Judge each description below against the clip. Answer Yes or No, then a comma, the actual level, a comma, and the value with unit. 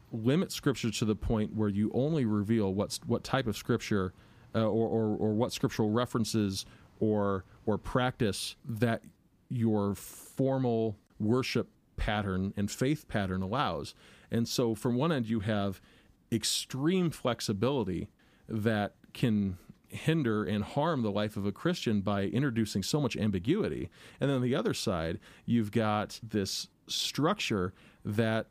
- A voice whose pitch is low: Yes, low, 110 Hz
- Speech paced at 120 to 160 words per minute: Yes, average, 145 wpm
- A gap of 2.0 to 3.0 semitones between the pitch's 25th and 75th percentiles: Yes, average, 2.7 semitones